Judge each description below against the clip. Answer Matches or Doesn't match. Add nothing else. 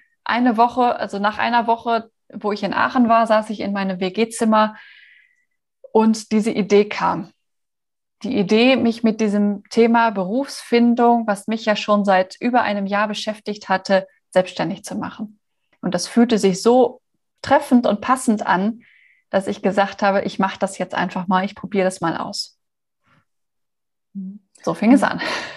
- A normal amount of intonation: Matches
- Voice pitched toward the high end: Matches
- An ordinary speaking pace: Matches